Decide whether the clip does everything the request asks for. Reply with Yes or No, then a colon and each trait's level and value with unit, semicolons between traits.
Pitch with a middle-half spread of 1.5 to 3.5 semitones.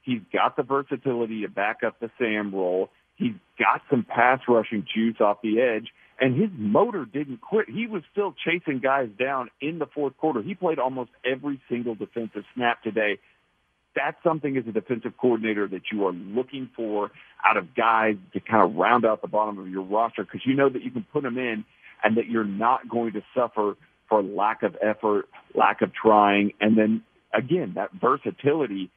No: average, 4.3 semitones